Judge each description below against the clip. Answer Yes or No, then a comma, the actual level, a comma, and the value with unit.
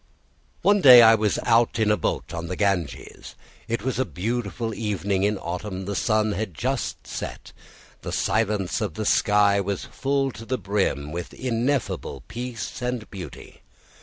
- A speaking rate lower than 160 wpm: No, average, 165 wpm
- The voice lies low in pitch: Yes, low, 105 Hz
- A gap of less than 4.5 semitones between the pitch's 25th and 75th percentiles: Yes, average, 3.4 semitones